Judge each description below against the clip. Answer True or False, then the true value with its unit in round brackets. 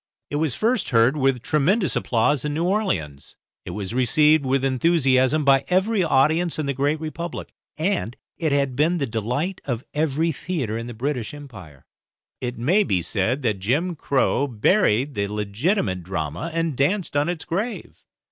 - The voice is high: False (140 Hz)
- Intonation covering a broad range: True (5.8 semitones)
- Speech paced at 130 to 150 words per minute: False (165 wpm)